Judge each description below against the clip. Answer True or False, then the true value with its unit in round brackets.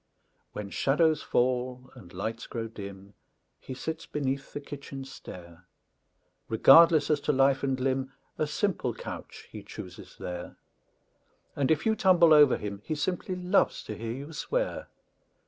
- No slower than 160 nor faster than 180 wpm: False (145 wpm)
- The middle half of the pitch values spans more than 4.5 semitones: True (5.4 semitones)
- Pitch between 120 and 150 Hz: True (135 Hz)